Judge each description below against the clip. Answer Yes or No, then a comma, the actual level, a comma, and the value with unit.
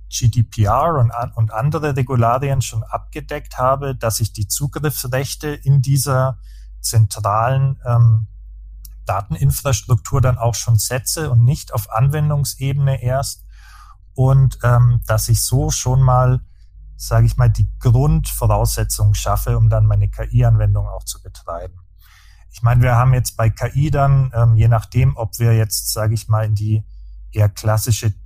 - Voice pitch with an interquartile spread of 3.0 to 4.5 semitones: Yes, average, 3.8 semitones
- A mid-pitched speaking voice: No, low, 115 Hz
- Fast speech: No, average, 140 wpm